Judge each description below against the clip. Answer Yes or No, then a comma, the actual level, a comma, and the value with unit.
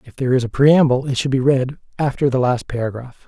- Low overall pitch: Yes, low, 130 Hz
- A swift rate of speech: Yes, fast, 240 wpm